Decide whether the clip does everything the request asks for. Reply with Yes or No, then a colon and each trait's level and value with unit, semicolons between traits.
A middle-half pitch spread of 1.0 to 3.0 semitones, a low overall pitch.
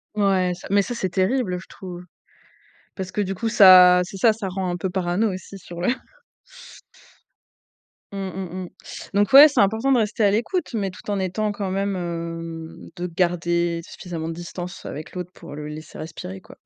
No: narrow, 2.6 semitones; medium, 185 Hz